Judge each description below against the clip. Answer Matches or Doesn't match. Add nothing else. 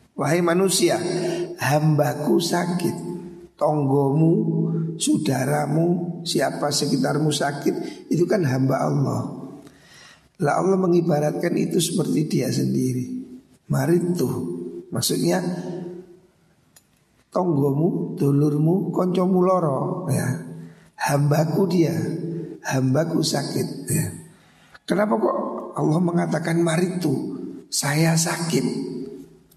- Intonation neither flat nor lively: Matches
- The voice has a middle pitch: Matches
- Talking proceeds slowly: Matches